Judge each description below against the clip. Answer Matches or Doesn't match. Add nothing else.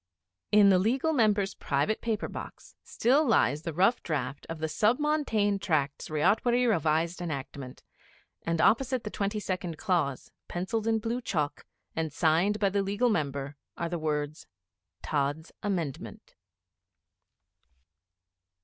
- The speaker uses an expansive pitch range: Matches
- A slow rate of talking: Matches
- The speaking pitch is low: Doesn't match